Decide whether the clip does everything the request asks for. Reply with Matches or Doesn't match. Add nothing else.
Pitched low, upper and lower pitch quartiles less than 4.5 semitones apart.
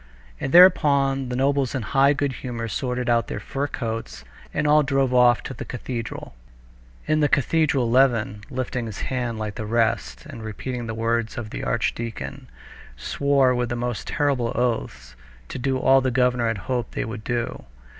Matches